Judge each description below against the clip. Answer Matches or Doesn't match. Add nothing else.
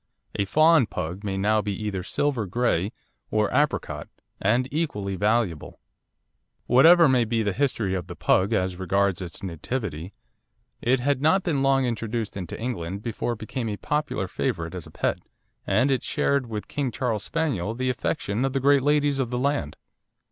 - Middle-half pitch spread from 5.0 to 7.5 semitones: Matches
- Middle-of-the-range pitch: Doesn't match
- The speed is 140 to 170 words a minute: Doesn't match